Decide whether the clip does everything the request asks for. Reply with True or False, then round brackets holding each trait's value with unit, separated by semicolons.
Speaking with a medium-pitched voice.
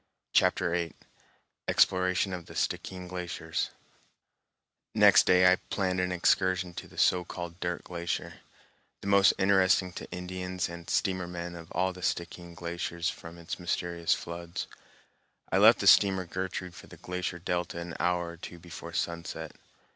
False (90 Hz)